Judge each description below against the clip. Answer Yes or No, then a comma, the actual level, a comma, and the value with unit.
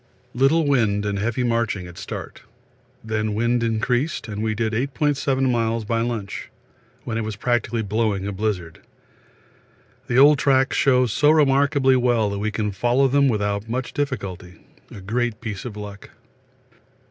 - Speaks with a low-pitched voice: Yes, low, 115 Hz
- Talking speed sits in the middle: Yes, average, 155 wpm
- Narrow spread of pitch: No, average, 3.8 semitones